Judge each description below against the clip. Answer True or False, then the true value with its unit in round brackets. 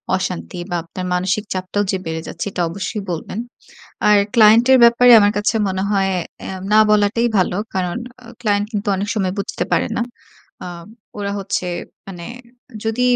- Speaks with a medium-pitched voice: False (200 Hz)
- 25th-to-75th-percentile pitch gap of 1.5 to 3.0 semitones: True (2.6 semitones)